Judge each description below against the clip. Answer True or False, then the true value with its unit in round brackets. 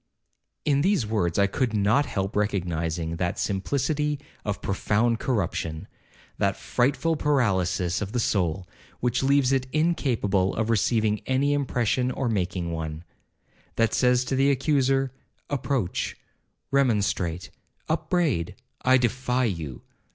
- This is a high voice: False (115 Hz)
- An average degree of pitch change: False (6.0 semitones)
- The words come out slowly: True (115 wpm)